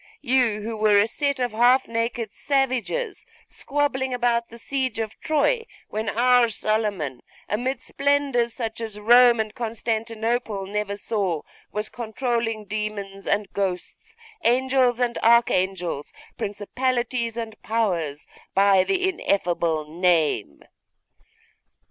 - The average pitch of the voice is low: No, high, 225 Hz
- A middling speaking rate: No, slow, 115 wpm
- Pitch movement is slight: No, average, 3.4 semitones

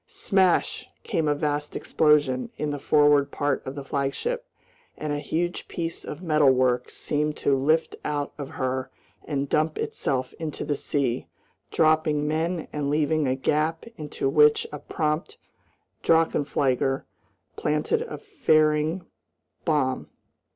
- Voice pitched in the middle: Yes, medium, 150 Hz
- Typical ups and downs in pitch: No, narrow, 2.1 semitones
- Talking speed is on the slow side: Yes, slow, 130 wpm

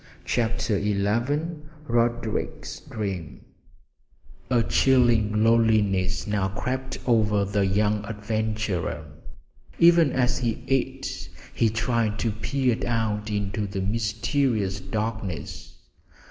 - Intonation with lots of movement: No, narrow, 2.6 semitones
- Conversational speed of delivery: No, slow, 95 wpm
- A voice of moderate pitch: No, low, 110 Hz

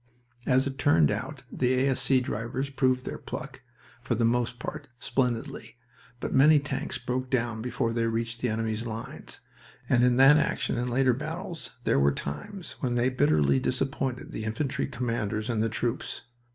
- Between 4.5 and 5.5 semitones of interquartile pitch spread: No, average, 2.7 semitones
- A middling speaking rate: Yes, average, 165 wpm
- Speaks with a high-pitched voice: No, low, 125 Hz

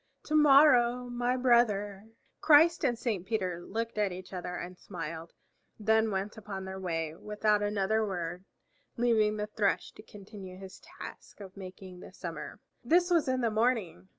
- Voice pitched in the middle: No, high, 210 Hz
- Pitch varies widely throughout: No, average, 4.1 semitones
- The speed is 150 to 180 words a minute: Yes, average, 160 wpm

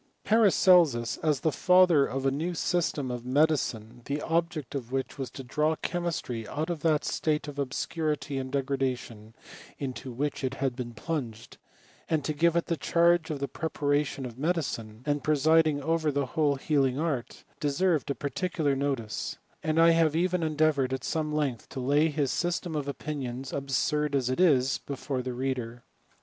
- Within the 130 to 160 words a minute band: No, average, 170 wpm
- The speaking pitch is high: No, medium, 145 Hz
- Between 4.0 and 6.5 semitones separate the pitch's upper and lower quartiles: No, average, 3.4 semitones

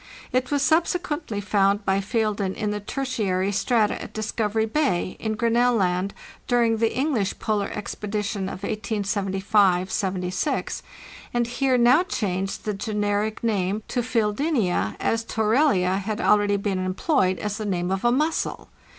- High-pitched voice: Yes, high, 210 Hz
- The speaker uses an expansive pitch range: No, average, 3.4 semitones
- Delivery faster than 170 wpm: No, average, 140 wpm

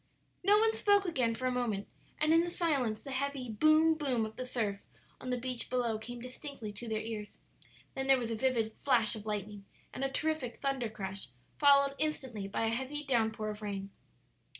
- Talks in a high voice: Yes, very high, 250 Hz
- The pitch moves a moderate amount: Yes, average, 4.3 semitones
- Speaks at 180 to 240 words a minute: Yes, average, 200 wpm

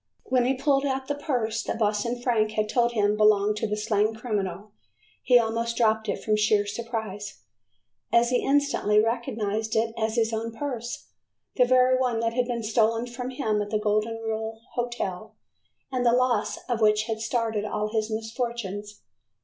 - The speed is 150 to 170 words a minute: No, average, 180 wpm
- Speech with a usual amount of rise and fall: No, narrow, 2.2 semitones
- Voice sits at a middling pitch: No, high, 225 Hz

